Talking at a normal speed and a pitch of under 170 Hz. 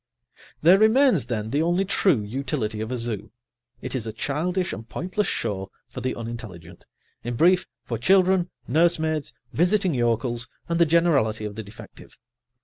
Yes: average, 155 wpm; medium, 140 Hz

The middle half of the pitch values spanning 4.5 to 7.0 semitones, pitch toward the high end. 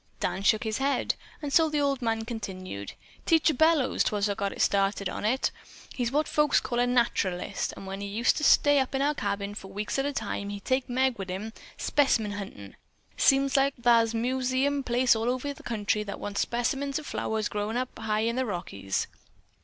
Yes: average, 4.9 semitones; high, 235 Hz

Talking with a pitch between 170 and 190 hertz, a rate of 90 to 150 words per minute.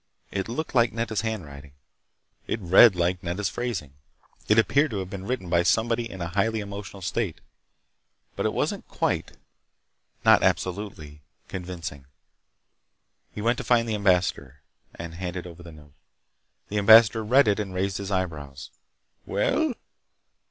No: very low, 95 Hz; average, 140 wpm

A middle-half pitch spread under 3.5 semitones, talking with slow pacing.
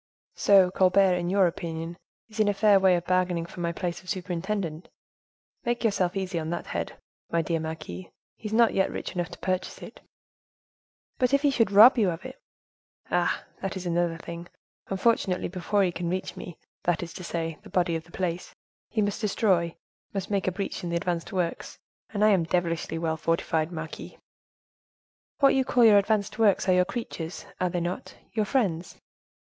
No: average, 3.1 semitones; average, 190 wpm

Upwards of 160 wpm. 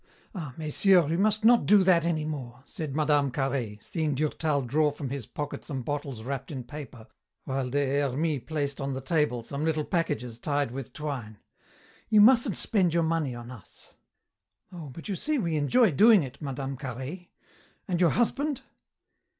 Yes: average, 175 wpm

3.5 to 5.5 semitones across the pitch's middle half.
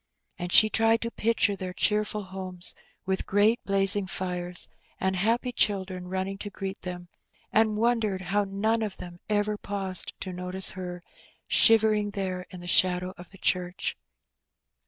No: narrow, 2.6 semitones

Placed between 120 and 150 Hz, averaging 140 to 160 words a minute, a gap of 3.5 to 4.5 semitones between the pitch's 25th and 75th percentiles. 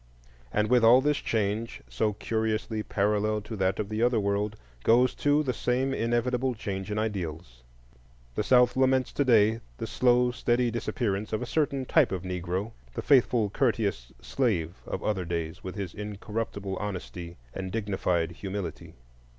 No: low, 105 Hz; average, 155 wpm; average, 4.2 semitones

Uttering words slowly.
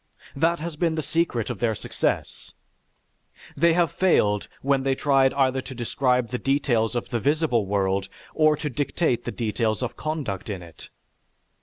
No: average, 165 wpm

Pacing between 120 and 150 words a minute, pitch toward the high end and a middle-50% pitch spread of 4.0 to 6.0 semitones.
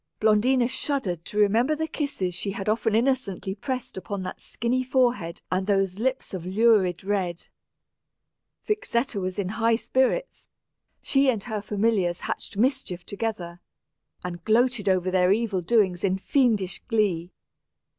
Yes: average, 140 wpm; high, 210 Hz; average, 4.7 semitones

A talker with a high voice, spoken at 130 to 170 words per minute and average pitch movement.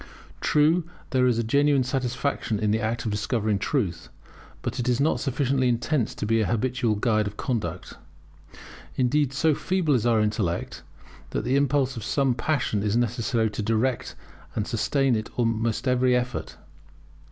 No: low, 120 Hz; average, 165 wpm; average, 3.6 semitones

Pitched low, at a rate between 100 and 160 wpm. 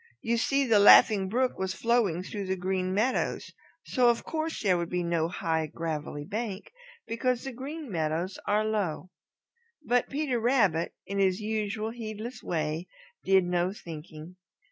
No: high, 200 Hz; average, 155 wpm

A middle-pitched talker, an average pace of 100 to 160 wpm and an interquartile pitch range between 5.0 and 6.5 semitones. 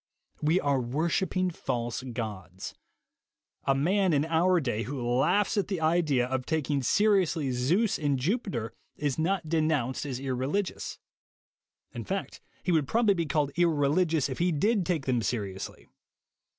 Yes: medium, 150 Hz; average, 150 wpm; wide, 5.4 semitones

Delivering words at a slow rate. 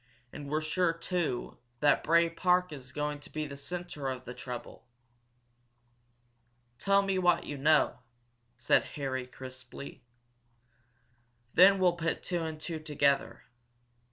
Yes: slow, 130 wpm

